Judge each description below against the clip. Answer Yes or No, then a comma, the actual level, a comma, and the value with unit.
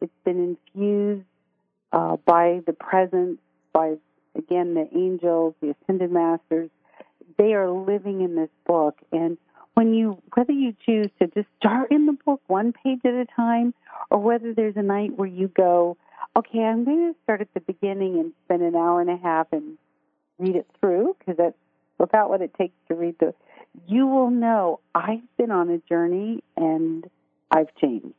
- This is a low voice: No, high, 190 Hz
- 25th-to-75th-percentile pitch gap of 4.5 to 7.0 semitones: Yes, average, 5.2 semitones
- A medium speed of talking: Yes, average, 180 wpm